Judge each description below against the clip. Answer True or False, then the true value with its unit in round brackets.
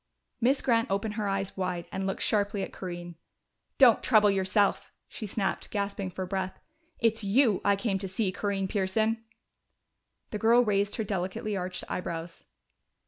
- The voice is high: True (200 Hz)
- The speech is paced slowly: False (155 wpm)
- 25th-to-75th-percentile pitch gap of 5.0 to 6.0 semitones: False (2.5 semitones)